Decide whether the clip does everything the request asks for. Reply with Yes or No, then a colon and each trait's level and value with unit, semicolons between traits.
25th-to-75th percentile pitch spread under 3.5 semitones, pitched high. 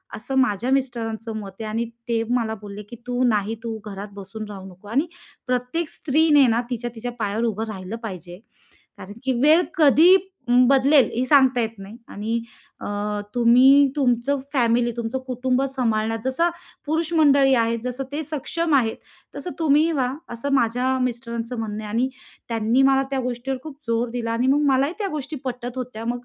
Yes: average, 3.1 semitones; high, 245 Hz